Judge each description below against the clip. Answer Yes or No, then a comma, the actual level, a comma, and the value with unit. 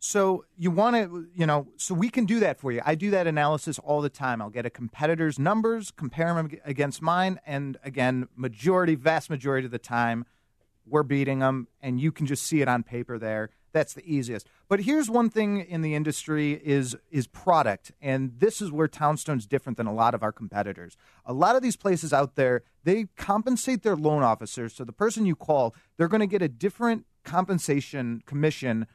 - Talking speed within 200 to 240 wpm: Yes, fast, 205 wpm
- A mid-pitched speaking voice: Yes, medium, 150 Hz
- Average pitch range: No, wide, 6.2 semitones